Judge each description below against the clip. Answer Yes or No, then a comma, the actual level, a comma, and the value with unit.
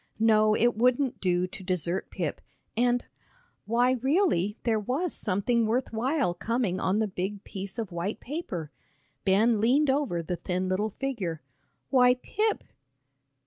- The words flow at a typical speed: Yes, average, 145 wpm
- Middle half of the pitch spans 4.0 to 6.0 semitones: Yes, average, 5.0 semitones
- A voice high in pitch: Yes, high, 220 Hz